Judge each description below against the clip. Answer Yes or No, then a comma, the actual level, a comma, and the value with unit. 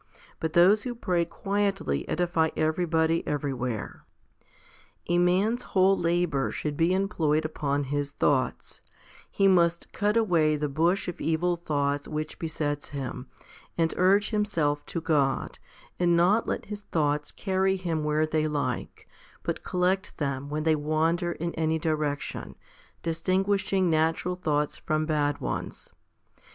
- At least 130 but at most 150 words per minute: Yes, average, 140 wpm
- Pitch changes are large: No, average, 3.5 semitones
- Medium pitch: Yes, medium, 160 Hz